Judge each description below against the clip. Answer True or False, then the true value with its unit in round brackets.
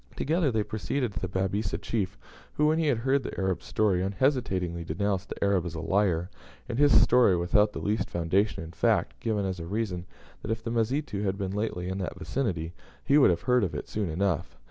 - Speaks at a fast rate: True (215 wpm)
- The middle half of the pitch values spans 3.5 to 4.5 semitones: True (4.1 semitones)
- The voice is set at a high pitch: False (100 Hz)